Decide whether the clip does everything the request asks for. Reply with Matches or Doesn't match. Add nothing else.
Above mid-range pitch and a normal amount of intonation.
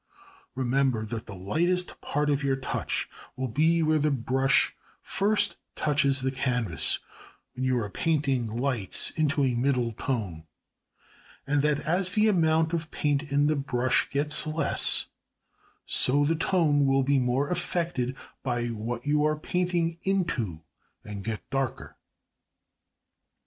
Doesn't match